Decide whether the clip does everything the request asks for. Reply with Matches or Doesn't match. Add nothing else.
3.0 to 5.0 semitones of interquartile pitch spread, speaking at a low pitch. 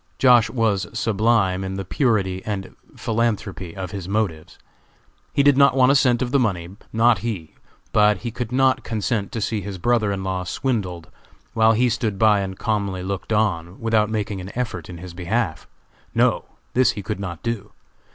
Matches